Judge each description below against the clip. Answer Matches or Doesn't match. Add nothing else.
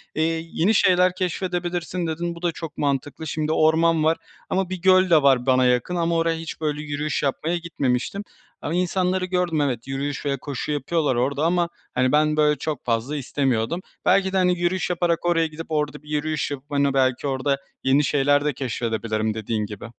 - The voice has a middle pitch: Matches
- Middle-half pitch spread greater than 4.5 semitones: Doesn't match